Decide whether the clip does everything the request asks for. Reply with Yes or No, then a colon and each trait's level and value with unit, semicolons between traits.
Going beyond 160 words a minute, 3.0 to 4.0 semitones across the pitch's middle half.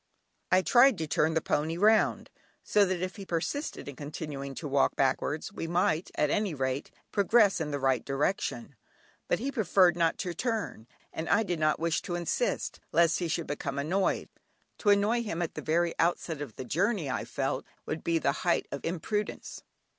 No: average, 190 wpm; average, 5.1 semitones